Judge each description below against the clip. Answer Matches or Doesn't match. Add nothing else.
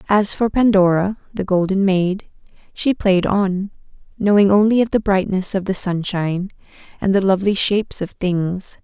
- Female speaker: Matches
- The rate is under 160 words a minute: Matches